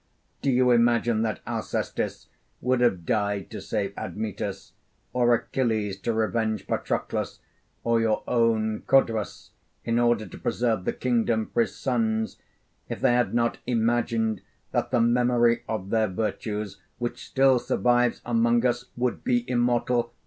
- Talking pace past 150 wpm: No, average, 140 wpm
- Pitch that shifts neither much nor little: No, narrow, 1.7 semitones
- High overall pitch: No, low, 115 Hz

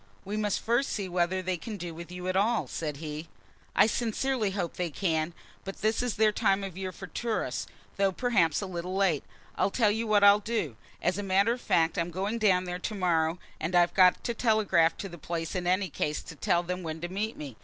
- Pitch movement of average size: Yes, average, 3.4 semitones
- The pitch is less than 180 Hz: No, medium, 185 Hz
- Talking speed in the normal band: No, fast, 230 wpm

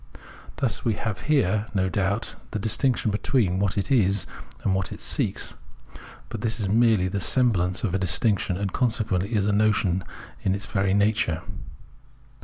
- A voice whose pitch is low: Yes, low, 100 Hz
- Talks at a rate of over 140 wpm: Yes, average, 170 wpm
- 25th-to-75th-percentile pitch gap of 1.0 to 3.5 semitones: Yes, average, 2.9 semitones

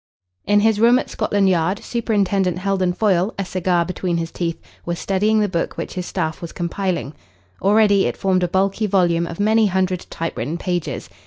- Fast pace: No, average, 180 wpm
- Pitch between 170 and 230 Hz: Yes, medium, 185 Hz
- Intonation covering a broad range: No, average, 2.8 semitones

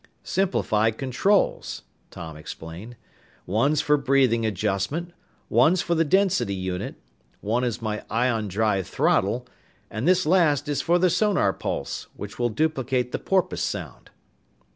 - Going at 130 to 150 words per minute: Yes, slow, 135 wpm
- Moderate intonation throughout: No, wide, 7.2 semitones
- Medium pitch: No, low, 125 Hz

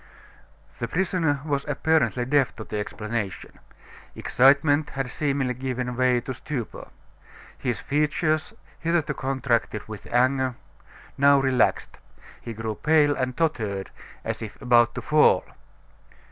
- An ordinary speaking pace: No, slow, 120 wpm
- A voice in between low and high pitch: No, low, 130 Hz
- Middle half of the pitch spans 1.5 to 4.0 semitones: Yes, average, 3.5 semitones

